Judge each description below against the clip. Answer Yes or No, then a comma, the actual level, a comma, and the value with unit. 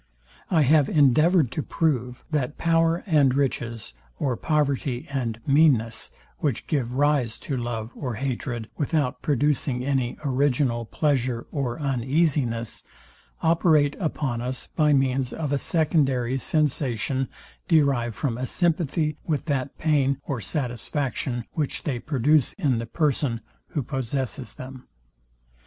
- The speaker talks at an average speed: No, slow, 125 wpm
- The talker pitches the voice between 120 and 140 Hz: Yes, low, 135 Hz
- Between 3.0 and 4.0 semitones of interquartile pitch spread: Yes, average, 3.5 semitones